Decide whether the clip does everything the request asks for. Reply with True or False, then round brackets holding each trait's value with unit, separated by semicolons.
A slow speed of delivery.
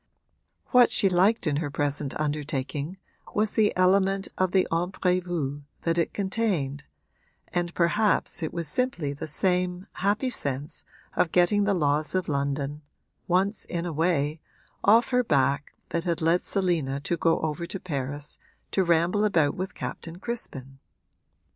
False (150 wpm)